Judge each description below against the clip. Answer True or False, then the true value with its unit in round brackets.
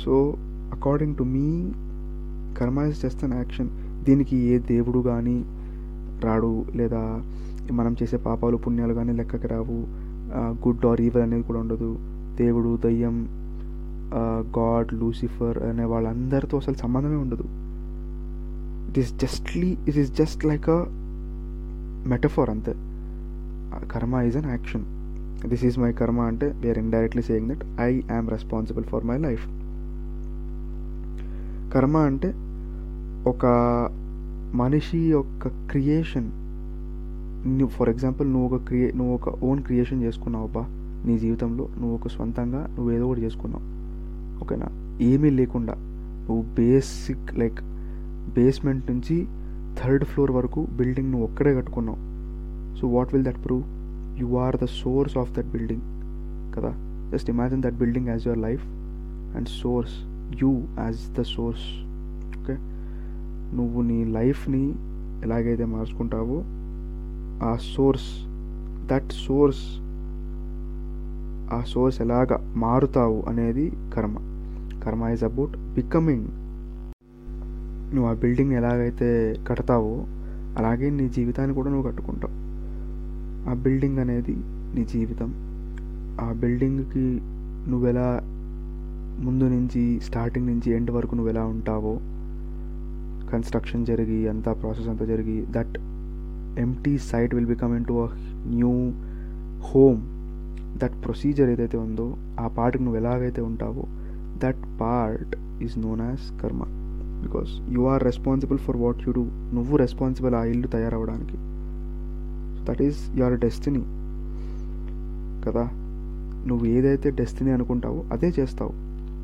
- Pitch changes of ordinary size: False (6.9 semitones)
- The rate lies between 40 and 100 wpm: False (115 wpm)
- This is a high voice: False (115 Hz)